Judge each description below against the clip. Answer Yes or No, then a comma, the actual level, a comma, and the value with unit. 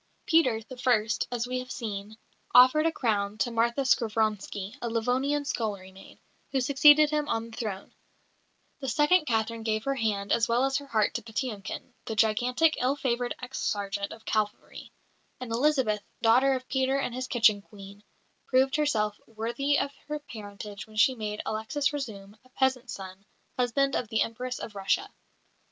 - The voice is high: Yes, high, 235 Hz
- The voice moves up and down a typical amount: Yes, average, 3.7 semitones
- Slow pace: No, average, 170 wpm